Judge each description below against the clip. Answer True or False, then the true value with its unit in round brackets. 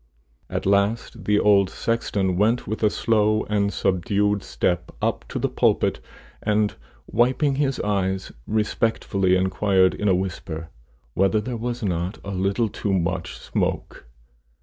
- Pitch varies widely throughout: False (2.4 semitones)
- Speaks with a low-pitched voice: True (100 Hz)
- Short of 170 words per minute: True (140 wpm)